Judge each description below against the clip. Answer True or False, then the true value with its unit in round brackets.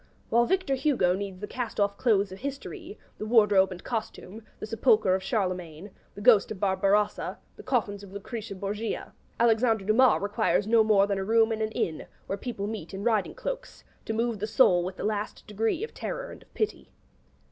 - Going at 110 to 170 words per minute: False (195 wpm)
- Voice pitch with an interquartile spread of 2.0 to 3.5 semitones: True (3.0 semitones)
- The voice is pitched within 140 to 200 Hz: False (215 Hz)